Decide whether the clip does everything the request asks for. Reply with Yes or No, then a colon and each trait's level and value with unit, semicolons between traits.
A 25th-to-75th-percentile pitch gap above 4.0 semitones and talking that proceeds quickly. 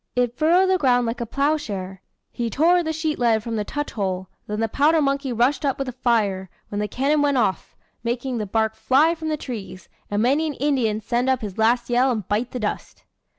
Yes: average, 4.8 semitones; fast, 225 wpm